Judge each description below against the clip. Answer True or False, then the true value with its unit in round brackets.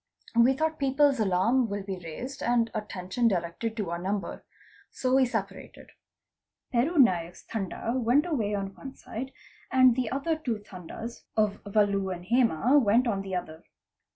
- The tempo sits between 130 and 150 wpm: False (160 wpm)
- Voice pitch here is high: True (225 Hz)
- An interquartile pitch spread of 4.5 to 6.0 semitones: True (4.9 semitones)